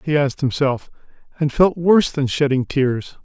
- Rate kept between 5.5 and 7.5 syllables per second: No, 5.0 syllables/s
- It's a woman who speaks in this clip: No, male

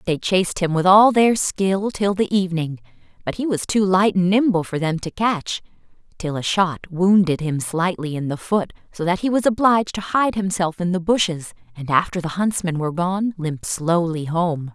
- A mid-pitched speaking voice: Yes, medium, 180 Hz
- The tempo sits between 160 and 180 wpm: No, fast, 205 wpm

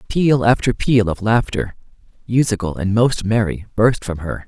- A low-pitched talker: Yes, low, 110 Hz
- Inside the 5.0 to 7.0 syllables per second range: No, 4.7 syllables/s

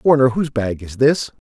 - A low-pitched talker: Yes, low, 130 Hz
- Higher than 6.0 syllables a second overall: No, 5.7 syllables/s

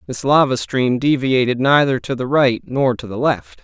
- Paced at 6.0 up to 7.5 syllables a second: No, 4.7 syllables/s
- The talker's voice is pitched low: Yes, low, 125 Hz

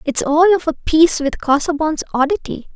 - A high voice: Yes, very high, 310 Hz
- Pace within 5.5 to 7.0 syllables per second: Yes, 5.7 syllables/s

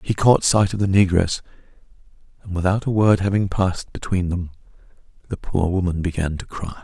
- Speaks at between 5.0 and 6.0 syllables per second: Yes, 5.5 syllables/s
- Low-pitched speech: Yes, very low, 95 Hz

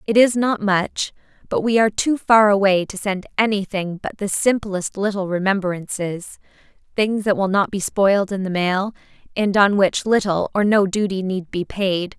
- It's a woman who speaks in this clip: Yes, female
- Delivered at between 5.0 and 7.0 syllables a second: No, 4.7 syllables/s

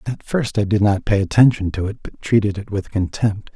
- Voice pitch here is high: No, low, 105 Hz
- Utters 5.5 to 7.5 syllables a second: No, 5.3 syllables/s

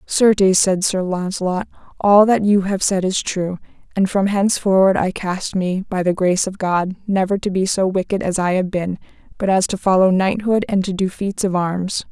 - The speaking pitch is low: No, high, 190 Hz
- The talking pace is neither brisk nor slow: No, fast, 210 wpm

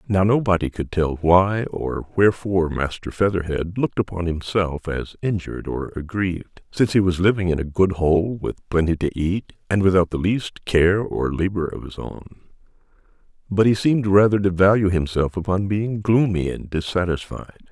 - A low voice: Yes, very low, 95 Hz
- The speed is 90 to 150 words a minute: No, average, 170 wpm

